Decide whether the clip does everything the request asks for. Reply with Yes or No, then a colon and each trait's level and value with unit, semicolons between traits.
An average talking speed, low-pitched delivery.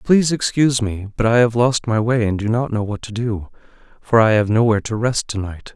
No: fast, 250 wpm; low, 115 Hz